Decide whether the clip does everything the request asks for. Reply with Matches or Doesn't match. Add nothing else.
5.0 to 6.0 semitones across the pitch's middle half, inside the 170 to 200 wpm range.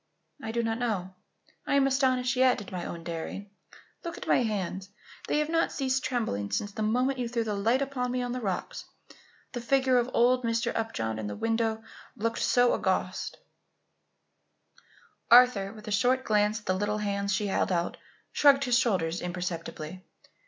Doesn't match